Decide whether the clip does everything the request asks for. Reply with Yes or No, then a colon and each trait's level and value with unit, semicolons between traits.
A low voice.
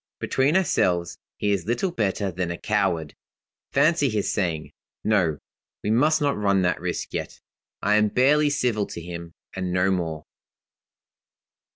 Yes: low, 100 Hz